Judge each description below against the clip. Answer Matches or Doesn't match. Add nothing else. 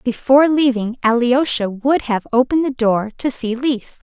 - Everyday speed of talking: Matches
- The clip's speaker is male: Doesn't match